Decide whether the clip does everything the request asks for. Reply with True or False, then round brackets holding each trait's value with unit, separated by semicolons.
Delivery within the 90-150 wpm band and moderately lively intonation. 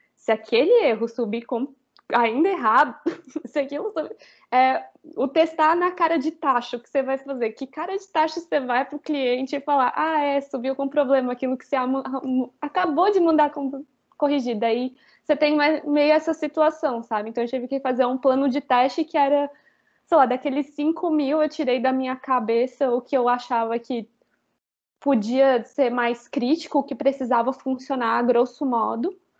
False (175 wpm; 3.2 semitones)